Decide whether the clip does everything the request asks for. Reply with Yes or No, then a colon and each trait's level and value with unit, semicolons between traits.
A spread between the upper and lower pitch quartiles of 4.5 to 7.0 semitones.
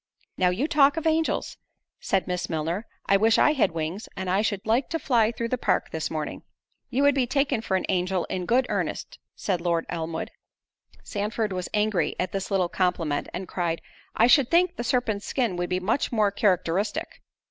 Yes: average, 5.3 semitones